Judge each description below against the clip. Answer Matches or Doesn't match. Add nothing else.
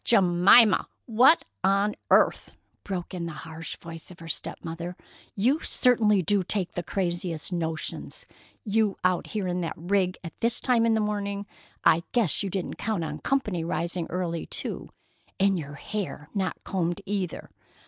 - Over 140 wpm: Matches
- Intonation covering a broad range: Doesn't match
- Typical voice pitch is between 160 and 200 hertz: Matches